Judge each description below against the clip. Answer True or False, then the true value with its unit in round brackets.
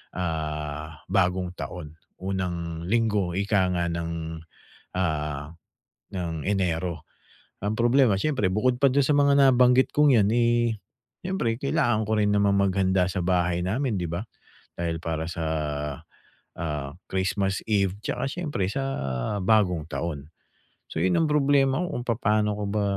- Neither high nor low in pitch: False (95 Hz)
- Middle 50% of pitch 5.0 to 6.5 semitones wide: True (5.5 semitones)